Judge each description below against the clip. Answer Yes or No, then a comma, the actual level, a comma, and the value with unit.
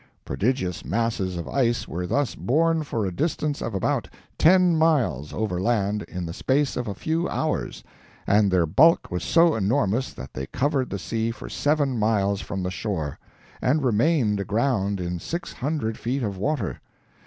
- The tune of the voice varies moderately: No, wide, 7.0 semitones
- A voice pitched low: Yes, low, 115 Hz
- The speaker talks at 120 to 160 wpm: No, average, 170 wpm